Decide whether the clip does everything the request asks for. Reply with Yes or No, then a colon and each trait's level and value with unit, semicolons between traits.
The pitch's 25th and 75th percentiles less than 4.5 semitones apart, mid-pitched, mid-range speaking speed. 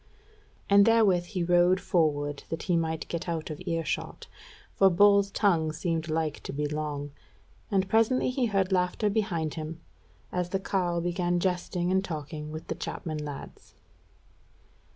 Yes: average, 3.4 semitones; medium, 175 Hz; average, 155 wpm